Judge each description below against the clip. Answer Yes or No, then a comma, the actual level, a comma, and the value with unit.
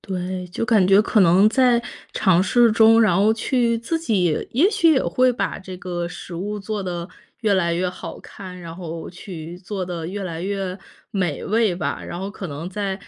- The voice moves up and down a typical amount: Yes, average, 3.7 semitones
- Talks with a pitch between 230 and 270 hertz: No, high, 190 Hz